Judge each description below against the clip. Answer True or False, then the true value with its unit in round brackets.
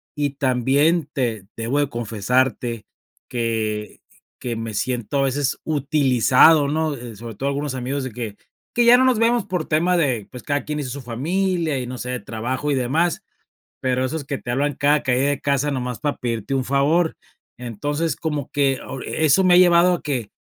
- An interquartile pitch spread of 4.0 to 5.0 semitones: False (3.6 semitones)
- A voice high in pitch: False (135 Hz)